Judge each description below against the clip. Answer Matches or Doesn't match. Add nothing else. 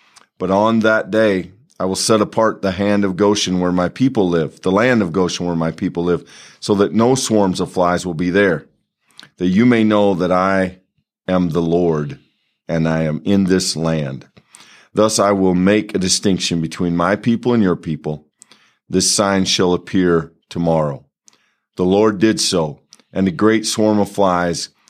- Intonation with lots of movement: Doesn't match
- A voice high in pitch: Doesn't match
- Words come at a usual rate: Matches